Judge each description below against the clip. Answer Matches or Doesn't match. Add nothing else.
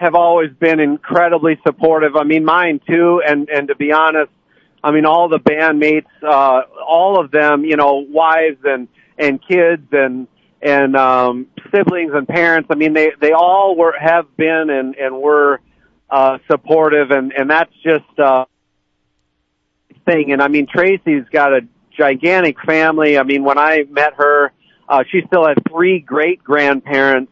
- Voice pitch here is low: Doesn't match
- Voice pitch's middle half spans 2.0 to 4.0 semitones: Matches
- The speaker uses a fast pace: Doesn't match